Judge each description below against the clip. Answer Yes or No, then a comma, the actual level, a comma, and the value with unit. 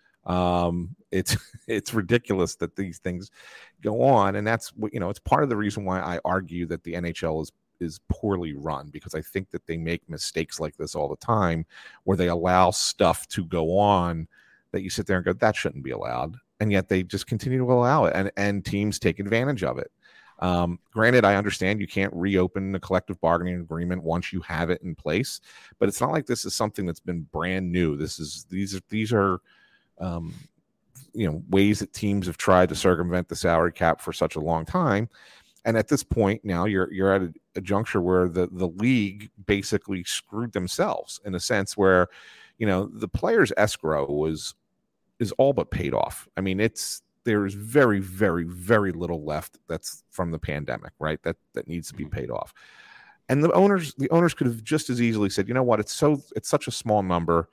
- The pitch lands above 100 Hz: No, very low, 95 Hz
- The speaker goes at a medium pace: No, fast, 210 wpm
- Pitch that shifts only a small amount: No, average, 3.4 semitones